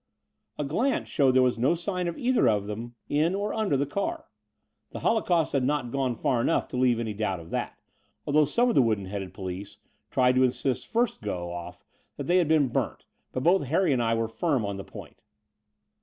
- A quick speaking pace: Yes, fast, 215 wpm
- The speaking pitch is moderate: No, low, 130 Hz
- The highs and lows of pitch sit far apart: Yes, wide, 7.1 semitones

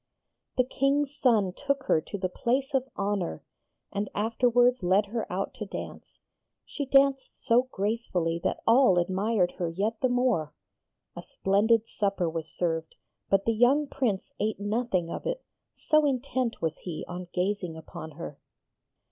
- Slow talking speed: No, average, 155 wpm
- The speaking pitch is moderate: No, high, 210 Hz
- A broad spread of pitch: Yes, wide, 5.7 semitones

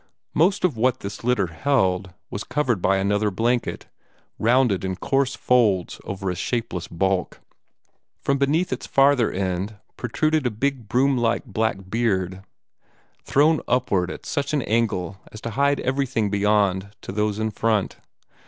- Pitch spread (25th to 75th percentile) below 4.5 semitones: No, average, 5.2 semitones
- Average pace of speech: Yes, average, 150 wpm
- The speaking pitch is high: No, low, 110 Hz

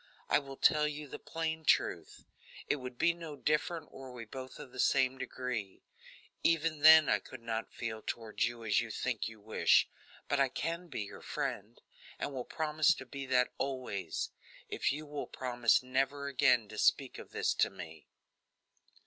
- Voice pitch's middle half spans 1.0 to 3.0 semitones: No, average, 3.8 semitones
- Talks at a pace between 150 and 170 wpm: No, average, 180 wpm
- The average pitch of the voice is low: Yes, low, 130 Hz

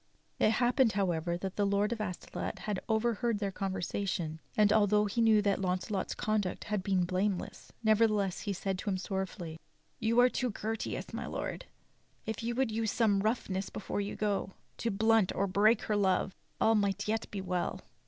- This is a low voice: No, high, 205 Hz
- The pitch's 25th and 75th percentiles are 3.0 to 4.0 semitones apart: No, narrow, 2.5 semitones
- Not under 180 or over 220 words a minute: Yes, average, 185 wpm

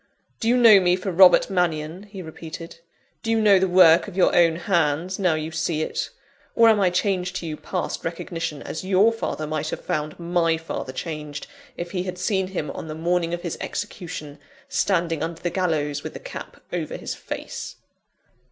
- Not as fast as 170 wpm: No, average, 195 wpm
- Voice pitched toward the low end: No, medium, 175 Hz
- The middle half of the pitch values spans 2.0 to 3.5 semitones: Yes, average, 2.8 semitones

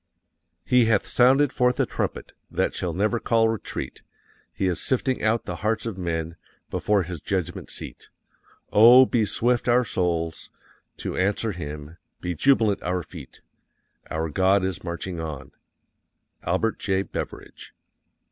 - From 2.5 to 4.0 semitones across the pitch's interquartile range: No, average, 5.0 semitones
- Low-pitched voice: Yes, very low, 95 Hz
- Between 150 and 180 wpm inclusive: No, average, 140 wpm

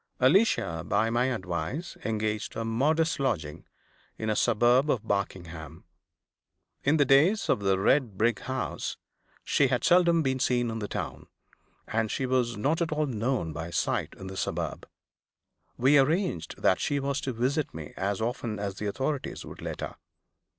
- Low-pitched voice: Yes, low, 120 Hz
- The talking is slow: No, average, 165 wpm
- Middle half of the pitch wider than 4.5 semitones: Yes, wide, 5.5 semitones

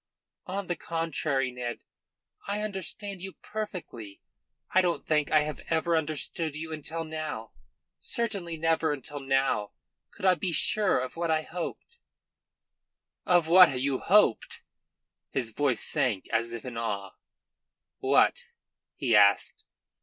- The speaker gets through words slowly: Yes, slow, 130 wpm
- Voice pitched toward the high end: No, medium, 155 Hz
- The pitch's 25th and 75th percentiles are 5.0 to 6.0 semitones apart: Yes, wide, 5.6 semitones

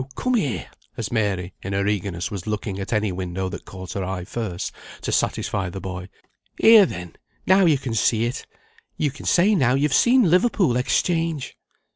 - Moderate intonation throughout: No, wide, 8.7 semitones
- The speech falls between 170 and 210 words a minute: Yes, average, 180 wpm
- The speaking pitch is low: Yes, low, 110 Hz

